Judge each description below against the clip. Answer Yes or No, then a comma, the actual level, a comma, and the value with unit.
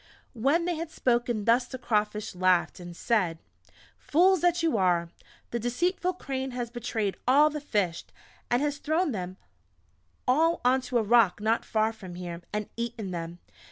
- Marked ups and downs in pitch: Yes, wide, 6.4 semitones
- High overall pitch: Yes, high, 235 Hz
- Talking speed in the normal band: Yes, average, 160 wpm